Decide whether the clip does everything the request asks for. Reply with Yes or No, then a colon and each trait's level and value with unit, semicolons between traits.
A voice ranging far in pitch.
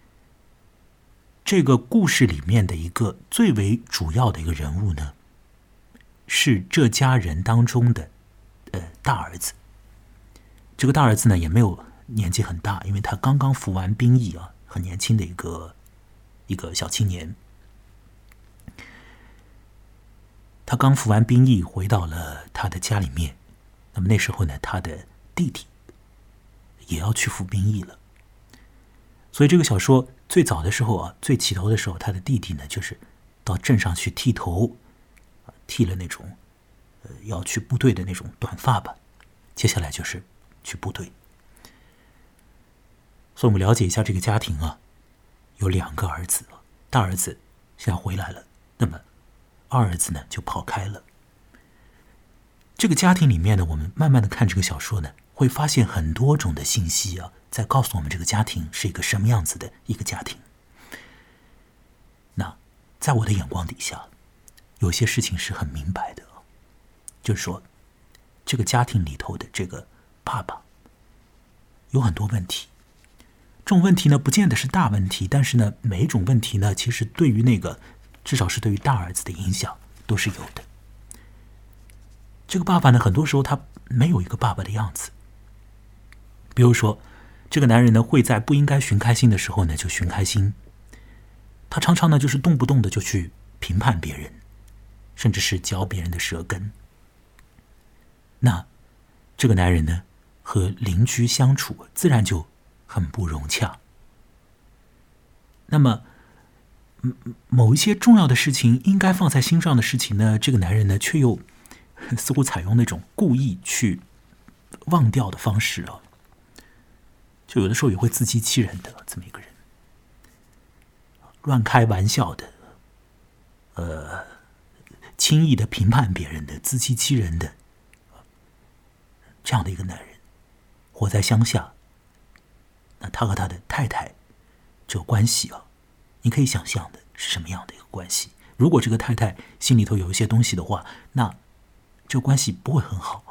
No: average, 4.2 semitones